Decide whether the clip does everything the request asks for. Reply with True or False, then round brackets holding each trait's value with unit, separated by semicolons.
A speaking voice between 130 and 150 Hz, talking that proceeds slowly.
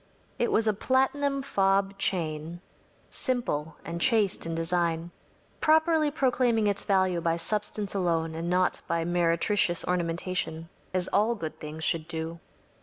False (180 Hz; 130 wpm)